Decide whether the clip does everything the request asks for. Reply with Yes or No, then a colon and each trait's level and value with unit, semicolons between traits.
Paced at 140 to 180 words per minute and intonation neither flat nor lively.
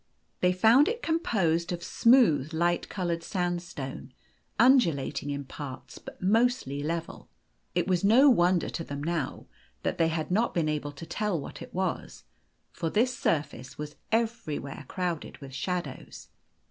No: average, 150 wpm; wide, 5.8 semitones